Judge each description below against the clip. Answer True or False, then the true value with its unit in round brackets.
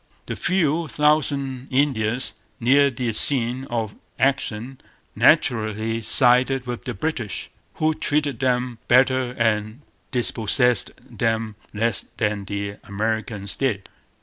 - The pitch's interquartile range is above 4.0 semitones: False (3.5 semitones)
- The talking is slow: True (110 wpm)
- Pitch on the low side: True (120 Hz)